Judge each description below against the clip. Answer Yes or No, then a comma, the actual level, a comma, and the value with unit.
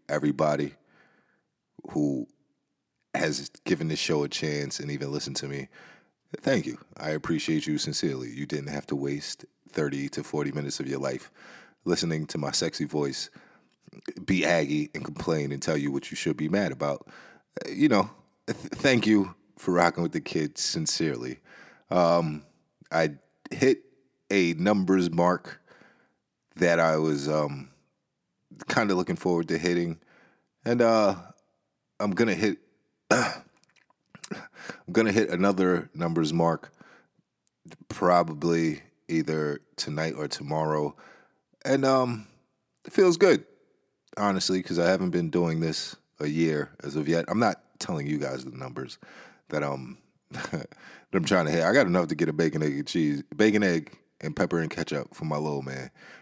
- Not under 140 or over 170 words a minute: Yes, average, 155 wpm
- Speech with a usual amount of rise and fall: Yes, average, 3.5 semitones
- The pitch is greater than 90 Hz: No, very low, 80 Hz